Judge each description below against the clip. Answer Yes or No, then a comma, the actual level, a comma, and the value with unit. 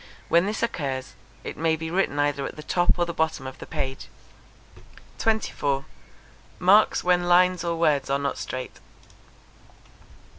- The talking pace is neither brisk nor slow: Yes, average, 150 wpm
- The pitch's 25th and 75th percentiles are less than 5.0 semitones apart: Yes, average, 4.2 semitones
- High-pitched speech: No, medium, 160 Hz